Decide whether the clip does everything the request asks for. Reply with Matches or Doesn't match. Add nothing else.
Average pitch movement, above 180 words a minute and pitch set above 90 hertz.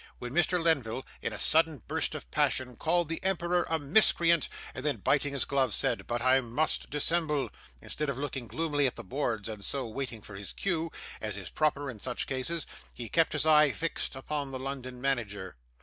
Matches